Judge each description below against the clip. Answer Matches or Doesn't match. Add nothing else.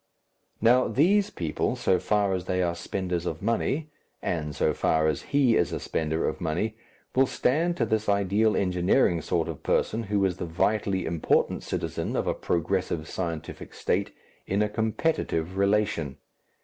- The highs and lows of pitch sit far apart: Doesn't match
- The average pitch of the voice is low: Matches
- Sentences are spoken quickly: Doesn't match